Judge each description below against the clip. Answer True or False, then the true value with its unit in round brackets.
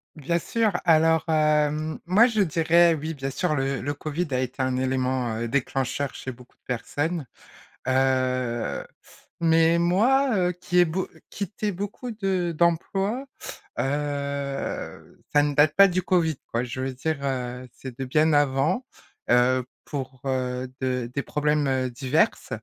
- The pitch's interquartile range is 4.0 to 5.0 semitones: True (4.7 semitones)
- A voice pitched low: False (145 Hz)